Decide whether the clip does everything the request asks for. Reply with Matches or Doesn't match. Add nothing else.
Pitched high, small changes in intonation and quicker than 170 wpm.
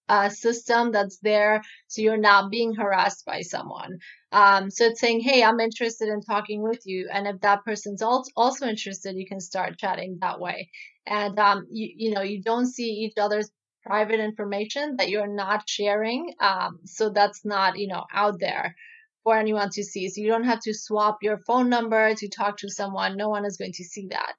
Matches